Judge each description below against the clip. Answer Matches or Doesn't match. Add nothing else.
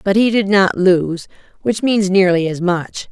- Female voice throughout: Matches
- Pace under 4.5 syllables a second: Matches